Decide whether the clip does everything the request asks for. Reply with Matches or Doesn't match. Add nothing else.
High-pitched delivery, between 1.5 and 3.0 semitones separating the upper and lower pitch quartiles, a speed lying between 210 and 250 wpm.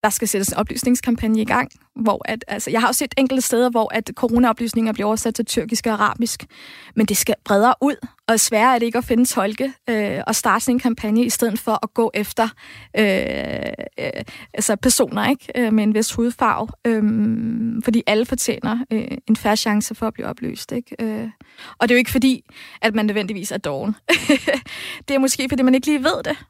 Matches